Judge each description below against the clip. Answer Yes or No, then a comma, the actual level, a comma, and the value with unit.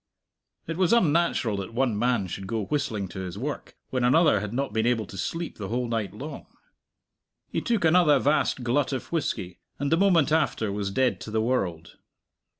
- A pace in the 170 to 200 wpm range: Yes, average, 190 wpm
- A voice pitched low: Yes, low, 125 Hz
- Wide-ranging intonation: Yes, wide, 6.4 semitones